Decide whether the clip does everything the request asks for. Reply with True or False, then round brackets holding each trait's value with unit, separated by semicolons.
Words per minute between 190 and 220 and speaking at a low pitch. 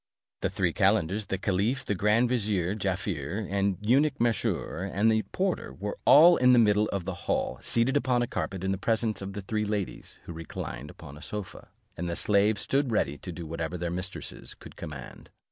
True (195 wpm; 100 Hz)